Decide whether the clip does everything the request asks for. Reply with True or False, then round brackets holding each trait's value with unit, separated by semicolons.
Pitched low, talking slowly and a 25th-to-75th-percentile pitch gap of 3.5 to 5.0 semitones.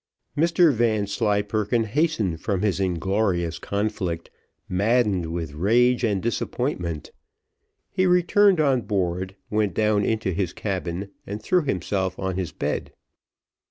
True (100 Hz; 120 wpm; 4.2 semitones)